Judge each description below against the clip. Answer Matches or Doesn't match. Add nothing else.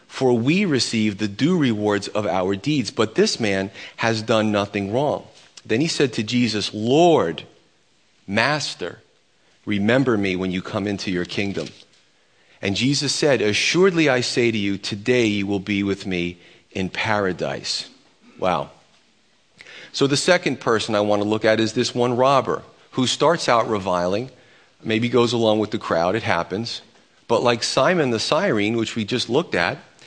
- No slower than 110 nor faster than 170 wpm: Matches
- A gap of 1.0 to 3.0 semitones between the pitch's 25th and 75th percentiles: Doesn't match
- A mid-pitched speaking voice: Doesn't match